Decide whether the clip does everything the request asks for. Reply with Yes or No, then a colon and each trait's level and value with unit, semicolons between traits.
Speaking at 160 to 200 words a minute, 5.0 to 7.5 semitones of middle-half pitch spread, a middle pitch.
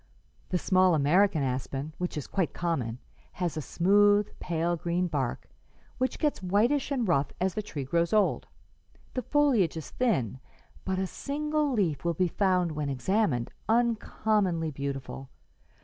No: average, 150 wpm; wide, 5.6 semitones; medium, 180 Hz